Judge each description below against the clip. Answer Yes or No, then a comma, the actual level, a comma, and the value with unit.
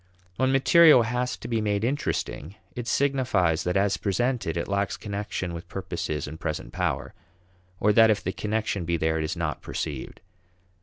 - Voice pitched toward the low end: Yes, low, 100 Hz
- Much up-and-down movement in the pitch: Yes, wide, 6.0 semitones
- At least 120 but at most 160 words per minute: No, average, 170 wpm